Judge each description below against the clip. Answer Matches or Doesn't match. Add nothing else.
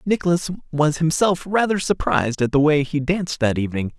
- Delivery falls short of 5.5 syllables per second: Doesn't match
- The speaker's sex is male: Matches